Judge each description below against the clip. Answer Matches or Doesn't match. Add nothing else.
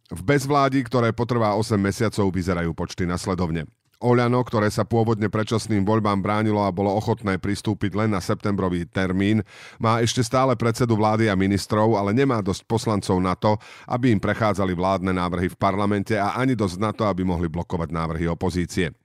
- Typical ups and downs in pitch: Matches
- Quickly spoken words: Matches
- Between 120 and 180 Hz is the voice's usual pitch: Doesn't match